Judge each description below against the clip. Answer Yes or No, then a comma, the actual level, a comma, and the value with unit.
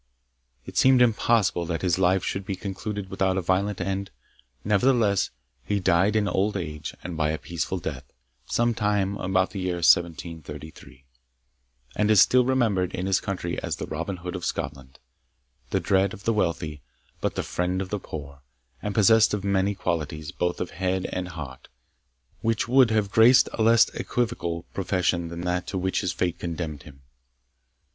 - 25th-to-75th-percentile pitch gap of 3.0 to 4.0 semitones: Yes, average, 3.3 semitones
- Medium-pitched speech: No, very low, 95 Hz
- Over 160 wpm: Yes, average, 170 wpm